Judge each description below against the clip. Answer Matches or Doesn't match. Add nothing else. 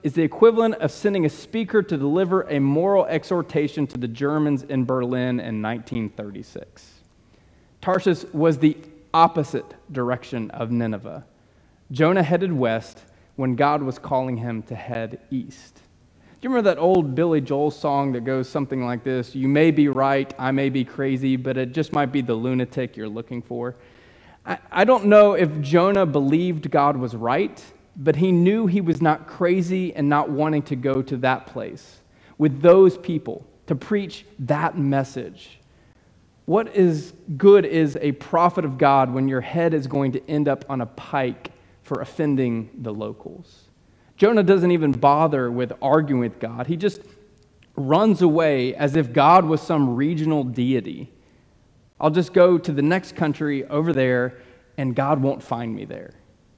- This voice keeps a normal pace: Matches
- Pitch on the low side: Doesn't match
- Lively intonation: Doesn't match